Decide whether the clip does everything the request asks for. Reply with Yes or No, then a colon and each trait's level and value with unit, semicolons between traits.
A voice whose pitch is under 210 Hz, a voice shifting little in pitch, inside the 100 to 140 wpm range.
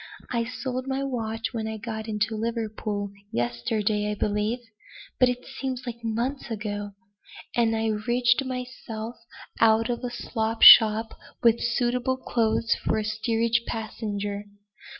No: high, 225 Hz; narrow, 2.0 semitones; slow, 135 wpm